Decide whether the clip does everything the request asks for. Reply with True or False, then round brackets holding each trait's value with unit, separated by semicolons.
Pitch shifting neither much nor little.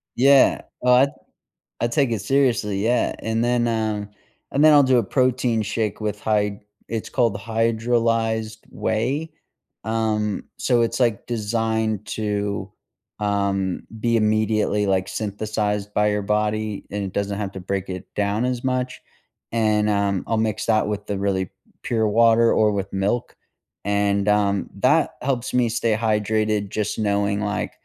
False (2.2 semitones)